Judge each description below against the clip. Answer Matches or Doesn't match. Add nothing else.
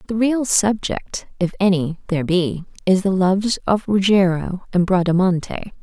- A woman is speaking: Matches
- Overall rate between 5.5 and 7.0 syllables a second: Doesn't match